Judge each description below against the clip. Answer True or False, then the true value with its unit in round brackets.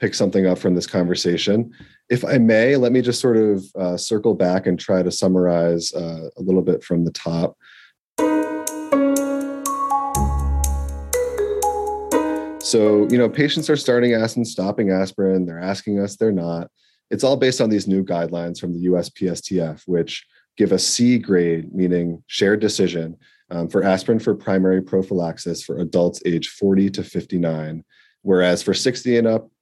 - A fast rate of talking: False (155 wpm)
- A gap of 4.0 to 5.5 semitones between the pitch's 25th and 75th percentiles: True (4.9 semitones)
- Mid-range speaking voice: False (95 Hz)